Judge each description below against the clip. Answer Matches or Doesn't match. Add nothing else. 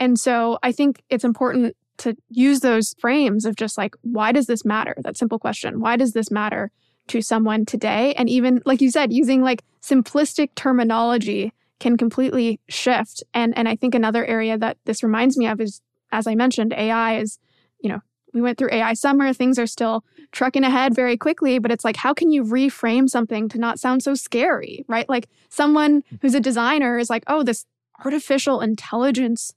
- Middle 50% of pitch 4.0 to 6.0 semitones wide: Doesn't match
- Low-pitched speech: Doesn't match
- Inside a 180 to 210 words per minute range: Matches